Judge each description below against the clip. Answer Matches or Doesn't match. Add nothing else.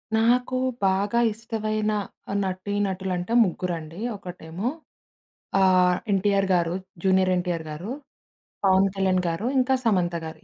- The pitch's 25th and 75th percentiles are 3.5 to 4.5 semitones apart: Doesn't match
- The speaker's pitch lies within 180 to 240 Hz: Matches